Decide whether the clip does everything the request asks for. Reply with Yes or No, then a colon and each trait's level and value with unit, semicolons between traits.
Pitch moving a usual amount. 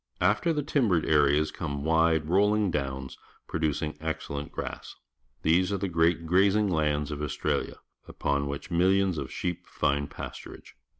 Yes: average, 4.1 semitones